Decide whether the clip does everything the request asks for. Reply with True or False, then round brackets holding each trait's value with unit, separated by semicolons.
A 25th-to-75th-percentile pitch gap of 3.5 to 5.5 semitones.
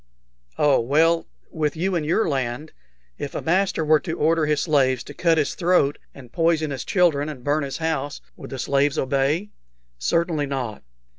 False (3.0 semitones)